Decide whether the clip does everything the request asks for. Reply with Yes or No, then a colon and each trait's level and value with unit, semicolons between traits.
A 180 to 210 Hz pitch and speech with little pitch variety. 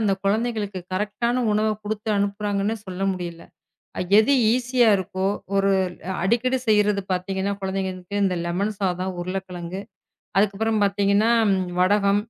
Yes: high, 200 Hz; narrow, 2.1 semitones